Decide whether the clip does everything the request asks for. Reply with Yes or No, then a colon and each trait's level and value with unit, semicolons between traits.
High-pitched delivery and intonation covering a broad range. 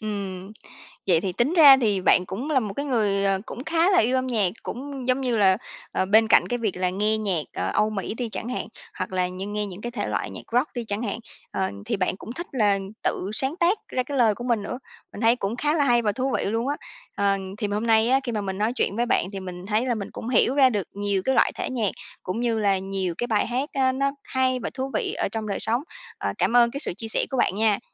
No: high, 225 Hz; average, 4.3 semitones